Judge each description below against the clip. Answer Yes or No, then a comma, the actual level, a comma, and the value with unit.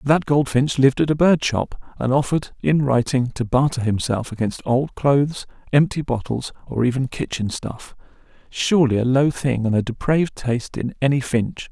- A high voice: No, low, 130 Hz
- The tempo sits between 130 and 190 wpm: Yes, average, 175 wpm